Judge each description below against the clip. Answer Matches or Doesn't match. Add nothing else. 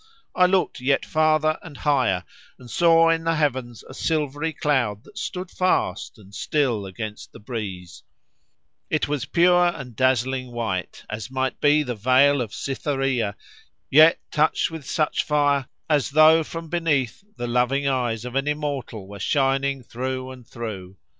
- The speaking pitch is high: Doesn't match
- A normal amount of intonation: Matches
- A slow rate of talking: Doesn't match